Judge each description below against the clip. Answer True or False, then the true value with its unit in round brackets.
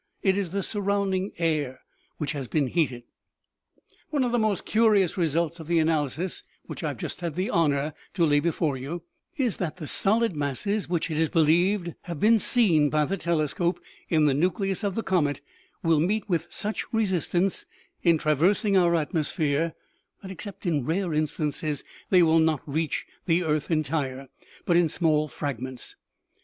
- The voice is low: False (165 Hz)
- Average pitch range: True (4.0 semitones)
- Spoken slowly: False (175 wpm)